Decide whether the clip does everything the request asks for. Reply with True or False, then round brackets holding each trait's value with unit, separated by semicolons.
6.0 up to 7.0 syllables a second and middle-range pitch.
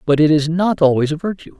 True (6.1 syllables/s; 160 Hz)